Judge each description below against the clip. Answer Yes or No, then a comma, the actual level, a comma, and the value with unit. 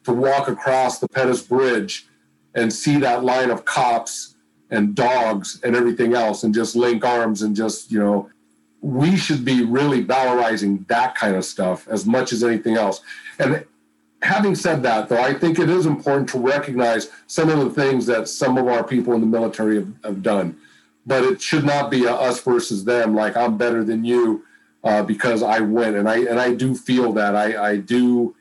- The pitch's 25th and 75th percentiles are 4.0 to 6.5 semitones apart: No, average, 3.3 semitones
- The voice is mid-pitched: No, low, 120 Hz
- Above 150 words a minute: Yes, average, 200 wpm